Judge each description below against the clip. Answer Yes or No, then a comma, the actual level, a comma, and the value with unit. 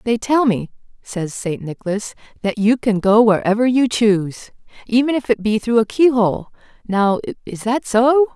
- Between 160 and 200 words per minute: Yes, average, 180 wpm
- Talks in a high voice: Yes, high, 225 Hz